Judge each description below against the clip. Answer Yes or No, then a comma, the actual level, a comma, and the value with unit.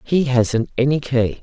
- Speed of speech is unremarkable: Yes, average, 170 wpm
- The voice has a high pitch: No, low, 130 Hz